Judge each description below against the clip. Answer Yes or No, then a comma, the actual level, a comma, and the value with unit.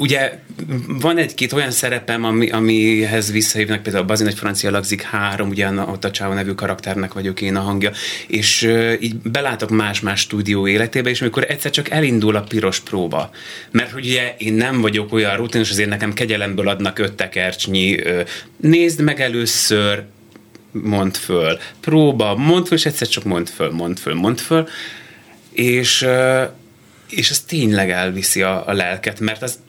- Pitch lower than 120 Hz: Yes, low, 110 Hz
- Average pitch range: Yes, average, 3.8 semitones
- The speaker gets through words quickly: Yes, fast, 165 wpm